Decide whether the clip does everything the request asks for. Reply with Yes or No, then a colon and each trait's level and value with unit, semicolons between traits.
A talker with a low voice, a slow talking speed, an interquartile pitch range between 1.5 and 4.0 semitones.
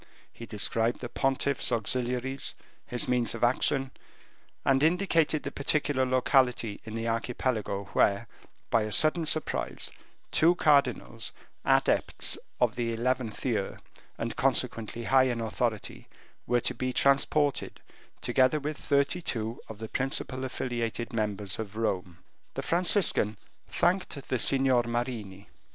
Yes: low, 125 Hz; slow, 130 wpm; average, 3.3 semitones